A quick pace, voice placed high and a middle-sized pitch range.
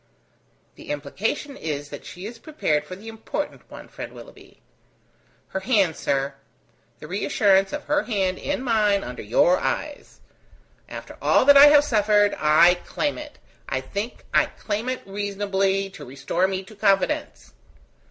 No: average, 150 wpm; high, 200 Hz; average, 4.5 semitones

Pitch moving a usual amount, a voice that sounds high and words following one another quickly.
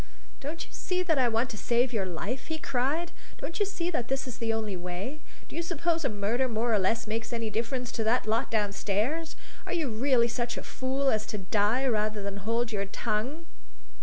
Yes: average, 4.3 semitones; high, 235 Hz; fast, 215 wpm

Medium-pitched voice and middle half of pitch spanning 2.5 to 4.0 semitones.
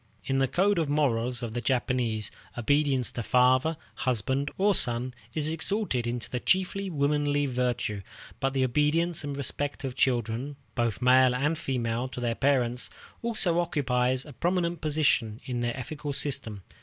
No: low, 130 Hz; average, 3.5 semitones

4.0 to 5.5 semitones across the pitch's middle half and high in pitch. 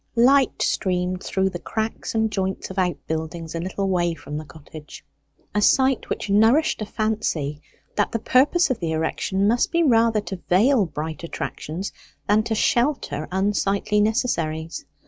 Yes: average, 5.1 semitones; high, 195 Hz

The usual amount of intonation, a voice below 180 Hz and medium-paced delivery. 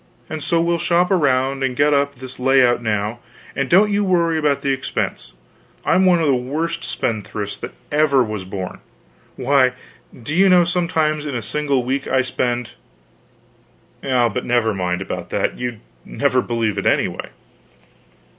Yes: average, 4.7 semitones; low, 135 Hz; average, 160 wpm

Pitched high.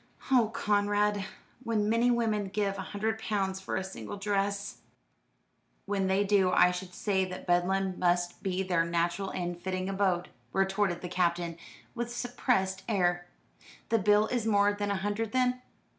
Yes: high, 195 Hz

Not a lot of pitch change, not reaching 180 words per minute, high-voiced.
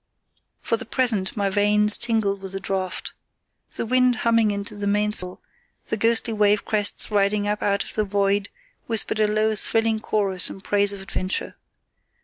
Yes: narrow, 1.6 semitones; average, 165 wpm; high, 205 Hz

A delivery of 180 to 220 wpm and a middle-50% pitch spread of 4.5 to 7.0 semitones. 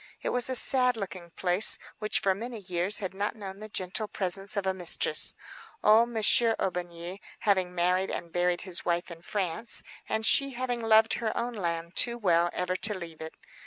No: average, 190 wpm; average, 3.9 semitones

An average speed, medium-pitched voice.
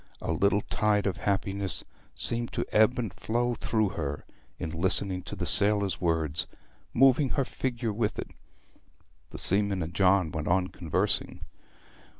No: average, 150 wpm; low, 100 Hz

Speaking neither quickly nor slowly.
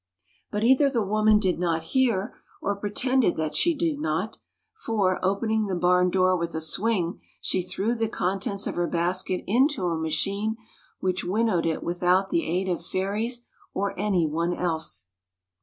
Yes: average, 170 wpm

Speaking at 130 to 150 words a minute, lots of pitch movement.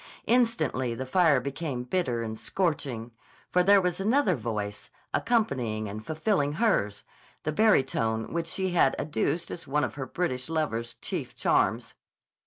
Yes: average, 145 wpm; wide, 7.2 semitones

